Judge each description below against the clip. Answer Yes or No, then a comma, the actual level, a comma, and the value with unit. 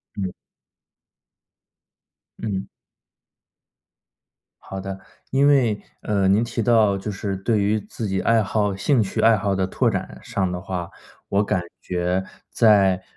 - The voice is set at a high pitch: No, low, 100 Hz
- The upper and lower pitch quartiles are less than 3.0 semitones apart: Yes, narrow, 2.5 semitones